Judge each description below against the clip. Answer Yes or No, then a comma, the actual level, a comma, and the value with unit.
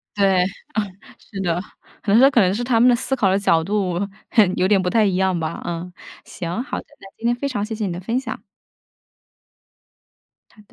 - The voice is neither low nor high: No, high, 200 Hz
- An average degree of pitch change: Yes, average, 4.1 semitones